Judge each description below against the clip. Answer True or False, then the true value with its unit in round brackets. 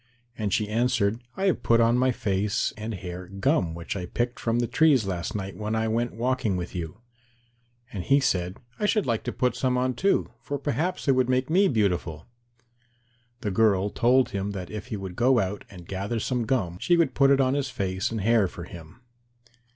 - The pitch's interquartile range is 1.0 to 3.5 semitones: False (4.9 semitones)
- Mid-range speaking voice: False (110 Hz)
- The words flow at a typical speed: False (210 wpm)